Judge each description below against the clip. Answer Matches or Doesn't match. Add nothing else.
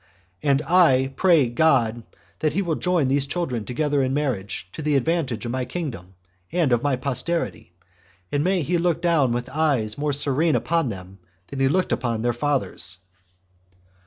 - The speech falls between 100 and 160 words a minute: Doesn't match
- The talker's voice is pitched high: Doesn't match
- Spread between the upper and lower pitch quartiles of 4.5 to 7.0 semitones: Matches